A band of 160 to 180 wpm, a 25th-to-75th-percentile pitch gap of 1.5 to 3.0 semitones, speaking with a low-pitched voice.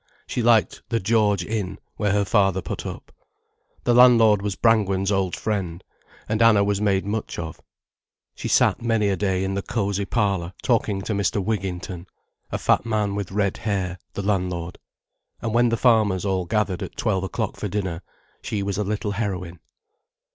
Yes: average, 175 wpm; narrow, 2.4 semitones; low, 100 Hz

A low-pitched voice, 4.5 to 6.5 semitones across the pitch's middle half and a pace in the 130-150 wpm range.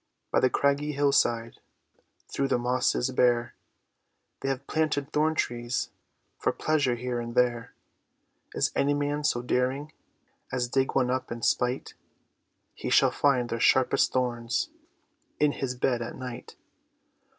No: low, 125 Hz; average, 2.7 semitones; average, 140 wpm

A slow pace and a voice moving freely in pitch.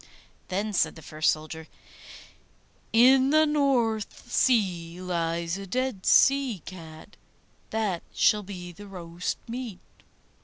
Yes: slow, 115 wpm; wide, 6.1 semitones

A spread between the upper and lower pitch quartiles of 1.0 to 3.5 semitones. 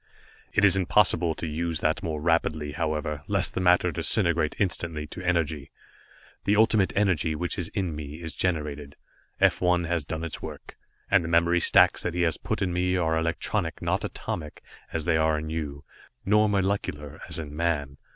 Yes: narrow, 2.6 semitones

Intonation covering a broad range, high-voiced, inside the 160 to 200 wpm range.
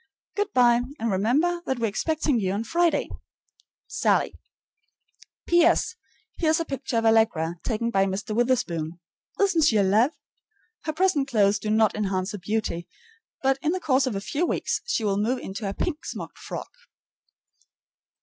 Yes: wide, 7.2 semitones; high, 235 Hz; average, 165 wpm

